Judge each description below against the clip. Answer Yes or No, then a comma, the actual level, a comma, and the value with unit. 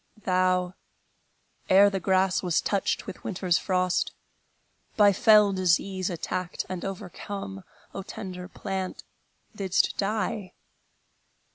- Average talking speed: No, slow, 105 wpm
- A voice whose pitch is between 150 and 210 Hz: Yes, high, 190 Hz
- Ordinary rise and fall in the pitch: No, narrow, 1.4 semitones